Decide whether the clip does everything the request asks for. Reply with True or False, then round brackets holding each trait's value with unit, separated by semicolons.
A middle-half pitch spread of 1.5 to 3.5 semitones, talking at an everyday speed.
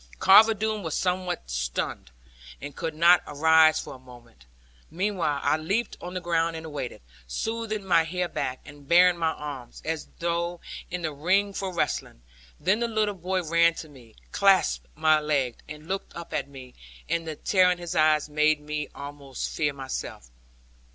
False (3.9 semitones; 175 wpm)